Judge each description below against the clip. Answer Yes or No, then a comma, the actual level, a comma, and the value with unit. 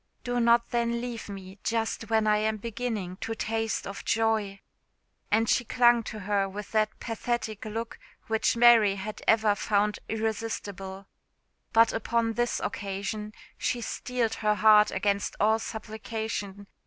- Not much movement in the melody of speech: Yes, narrow, 1.8 semitones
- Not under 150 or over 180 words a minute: No, average, 140 wpm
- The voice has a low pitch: No, high, 220 Hz